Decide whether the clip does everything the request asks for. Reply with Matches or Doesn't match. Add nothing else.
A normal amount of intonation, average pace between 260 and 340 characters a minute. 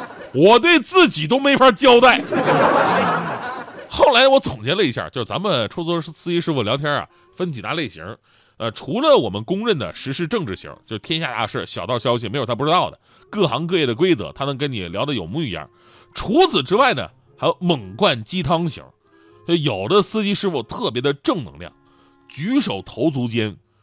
Doesn't match